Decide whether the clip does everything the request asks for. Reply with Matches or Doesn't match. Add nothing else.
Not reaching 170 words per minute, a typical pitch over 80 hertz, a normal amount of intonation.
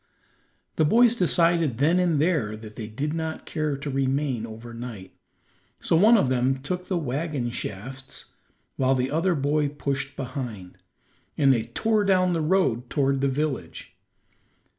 Matches